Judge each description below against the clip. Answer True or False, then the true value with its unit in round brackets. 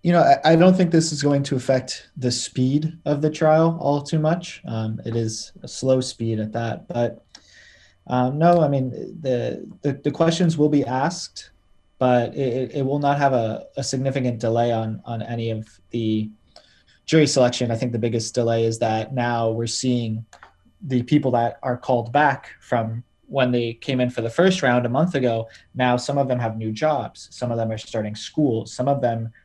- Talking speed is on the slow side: False (200 wpm)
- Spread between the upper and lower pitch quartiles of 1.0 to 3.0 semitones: False (3.9 semitones)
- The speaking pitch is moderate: False (125 Hz)